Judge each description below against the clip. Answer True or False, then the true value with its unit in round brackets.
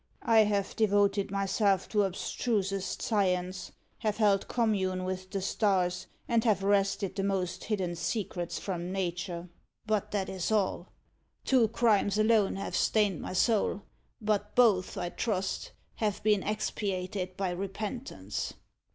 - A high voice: True (195 Hz)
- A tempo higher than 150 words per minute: False (135 wpm)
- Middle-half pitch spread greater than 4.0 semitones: False (2.4 semitones)